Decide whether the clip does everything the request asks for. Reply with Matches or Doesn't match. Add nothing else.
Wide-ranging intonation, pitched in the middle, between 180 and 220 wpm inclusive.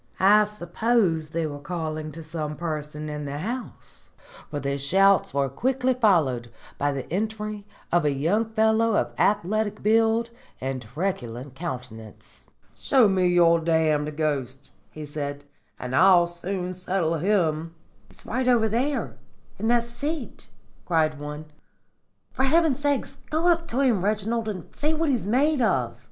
Doesn't match